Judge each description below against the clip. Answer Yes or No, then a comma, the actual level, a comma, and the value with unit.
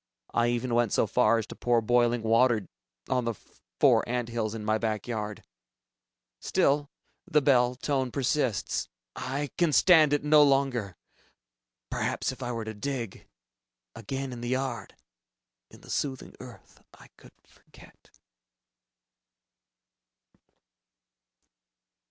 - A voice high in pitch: No, low, 120 Hz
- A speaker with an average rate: No, slow, 125 wpm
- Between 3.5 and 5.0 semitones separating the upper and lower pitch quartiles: No, average, 3.1 semitones